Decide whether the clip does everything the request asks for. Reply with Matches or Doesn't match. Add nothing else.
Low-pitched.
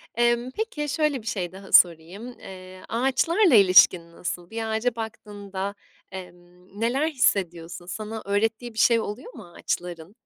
Doesn't match